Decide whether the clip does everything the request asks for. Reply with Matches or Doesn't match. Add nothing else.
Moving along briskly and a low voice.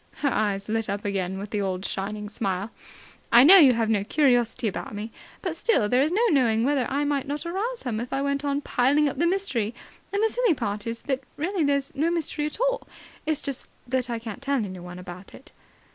Doesn't match